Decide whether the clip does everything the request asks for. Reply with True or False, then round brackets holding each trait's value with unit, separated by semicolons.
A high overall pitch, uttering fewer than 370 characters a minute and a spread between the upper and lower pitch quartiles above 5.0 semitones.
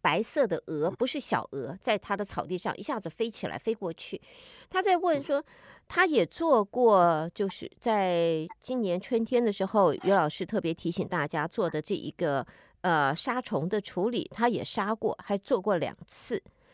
True (205 Hz; 250 characters per minute; 5.5 semitones)